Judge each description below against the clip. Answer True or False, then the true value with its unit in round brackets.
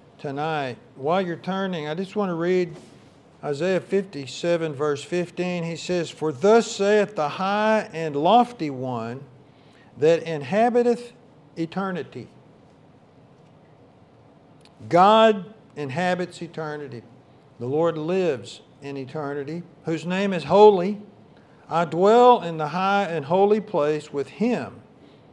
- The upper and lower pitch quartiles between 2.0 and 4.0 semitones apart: False (4.9 semitones)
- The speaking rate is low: True (115 wpm)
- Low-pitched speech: False (170 Hz)